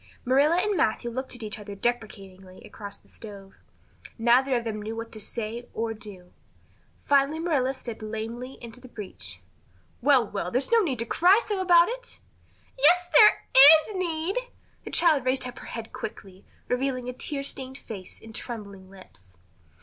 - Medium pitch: No, high, 245 Hz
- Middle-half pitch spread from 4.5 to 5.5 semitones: Yes, average, 4.9 semitones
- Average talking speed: Yes, average, 165 wpm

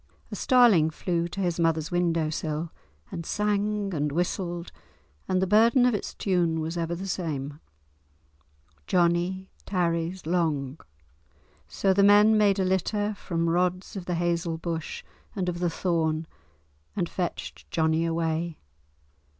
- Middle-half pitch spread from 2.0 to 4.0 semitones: Yes, average, 2.7 semitones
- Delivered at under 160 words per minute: Yes, average, 140 wpm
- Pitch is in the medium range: Yes, medium, 175 Hz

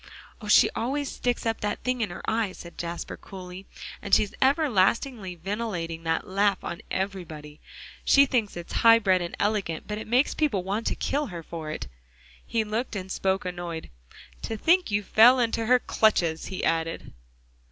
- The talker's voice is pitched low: No, high, 200 Hz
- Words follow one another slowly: No, average, 175 wpm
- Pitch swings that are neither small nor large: Yes, average, 4.6 semitones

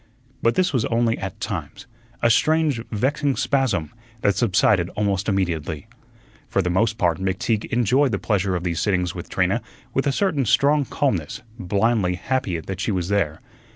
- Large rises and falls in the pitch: Yes, wide, 5.9 semitones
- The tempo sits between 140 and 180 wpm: Yes, average, 165 wpm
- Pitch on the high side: No, low, 105 Hz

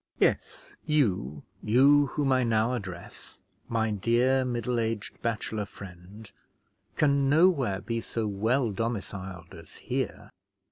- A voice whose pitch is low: Yes, low, 115 Hz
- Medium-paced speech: No, slow, 120 wpm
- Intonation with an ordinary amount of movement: Yes, average, 4.4 semitones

